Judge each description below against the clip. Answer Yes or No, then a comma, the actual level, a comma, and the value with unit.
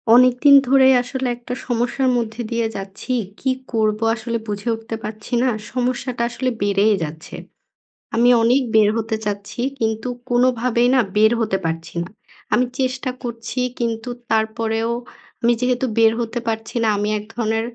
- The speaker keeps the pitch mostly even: Yes, narrow, 2.3 semitones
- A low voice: No, high, 230 Hz